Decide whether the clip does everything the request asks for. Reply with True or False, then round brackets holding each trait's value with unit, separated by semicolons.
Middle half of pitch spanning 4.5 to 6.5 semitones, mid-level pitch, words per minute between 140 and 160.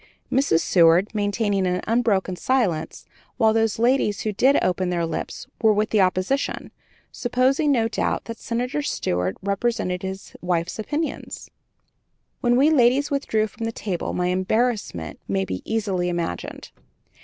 False (5.0 semitones; 210 Hz; 145 wpm)